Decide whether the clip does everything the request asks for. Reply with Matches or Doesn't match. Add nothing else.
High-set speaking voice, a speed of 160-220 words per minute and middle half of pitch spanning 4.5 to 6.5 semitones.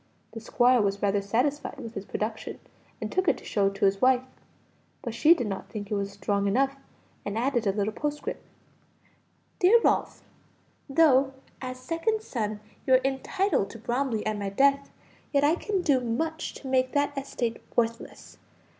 Matches